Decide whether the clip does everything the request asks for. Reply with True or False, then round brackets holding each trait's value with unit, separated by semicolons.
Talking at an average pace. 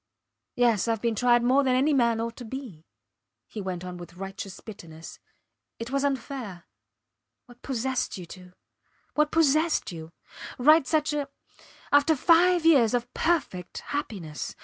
True (150 wpm)